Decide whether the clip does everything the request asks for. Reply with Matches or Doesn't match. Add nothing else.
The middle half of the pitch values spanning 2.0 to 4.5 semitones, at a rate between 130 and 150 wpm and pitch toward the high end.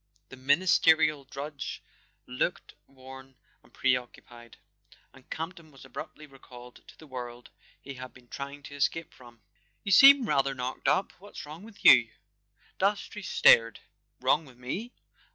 Doesn't match